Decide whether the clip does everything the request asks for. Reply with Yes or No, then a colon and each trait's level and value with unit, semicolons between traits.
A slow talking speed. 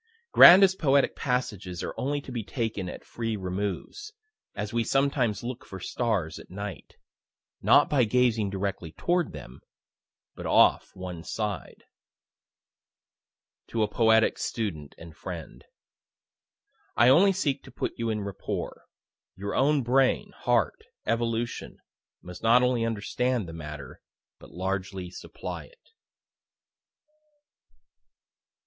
Yes: slow, 120 wpm